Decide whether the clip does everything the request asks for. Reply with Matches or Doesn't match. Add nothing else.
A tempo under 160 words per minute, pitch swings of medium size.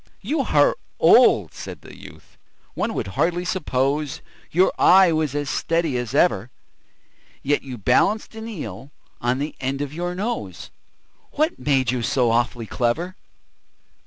Doesn't match